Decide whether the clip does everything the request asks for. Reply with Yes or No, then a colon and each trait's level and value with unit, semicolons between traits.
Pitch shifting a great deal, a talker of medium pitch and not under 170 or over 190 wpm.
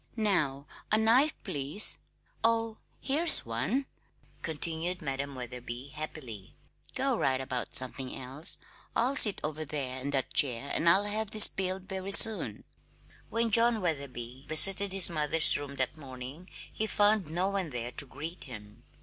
No: wide, 7.2 semitones; medium, 155 Hz; average, 150 wpm